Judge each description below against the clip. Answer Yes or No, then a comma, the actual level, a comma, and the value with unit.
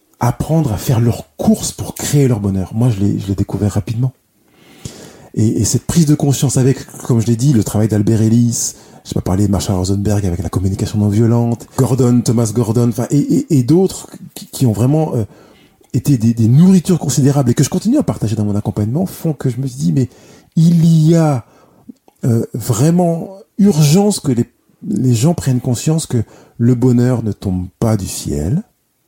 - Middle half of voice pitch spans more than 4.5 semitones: Yes, wide, 5.4 semitones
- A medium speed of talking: Yes, average, 195 wpm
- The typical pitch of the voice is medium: No, low, 125 Hz